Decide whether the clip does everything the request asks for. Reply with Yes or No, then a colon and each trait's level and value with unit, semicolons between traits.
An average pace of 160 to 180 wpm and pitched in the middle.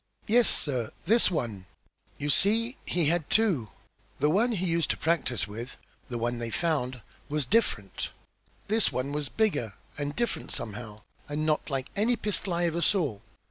Yes: average, 165 wpm; medium, 150 Hz